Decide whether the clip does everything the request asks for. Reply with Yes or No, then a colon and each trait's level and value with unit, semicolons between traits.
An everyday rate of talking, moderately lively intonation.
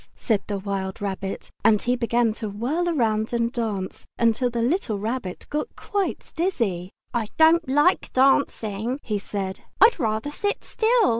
No: average, 155 wpm; wide, 5.7 semitones